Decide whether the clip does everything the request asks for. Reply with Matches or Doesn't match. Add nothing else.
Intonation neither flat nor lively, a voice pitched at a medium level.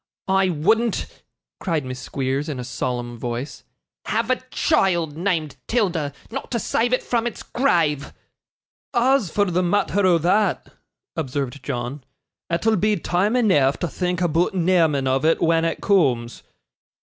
Doesn't match